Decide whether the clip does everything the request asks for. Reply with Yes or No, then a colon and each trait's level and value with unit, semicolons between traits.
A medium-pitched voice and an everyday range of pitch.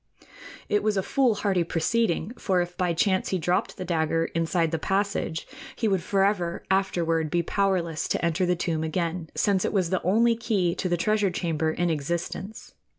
Yes: medium, 180 Hz; average, 3.0 semitones